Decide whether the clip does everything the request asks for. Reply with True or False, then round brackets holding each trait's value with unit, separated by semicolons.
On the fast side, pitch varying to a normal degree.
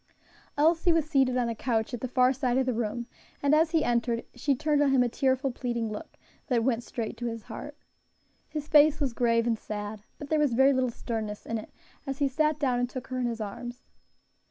True (230 wpm; 3.4 semitones)